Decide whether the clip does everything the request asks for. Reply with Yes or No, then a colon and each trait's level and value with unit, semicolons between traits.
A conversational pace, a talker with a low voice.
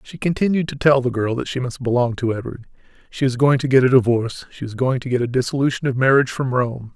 No: fast, 260 wpm; low, 130 Hz